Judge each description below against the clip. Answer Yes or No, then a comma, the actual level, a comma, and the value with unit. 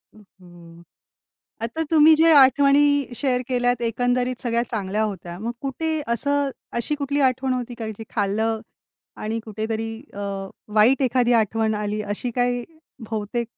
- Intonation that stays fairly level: No, average, 3.6 semitones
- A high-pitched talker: Yes, high, 235 Hz